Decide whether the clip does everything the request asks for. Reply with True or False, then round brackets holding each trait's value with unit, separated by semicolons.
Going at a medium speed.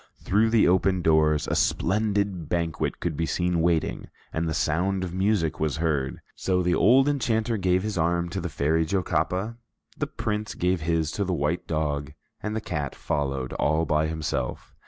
True (180 wpm)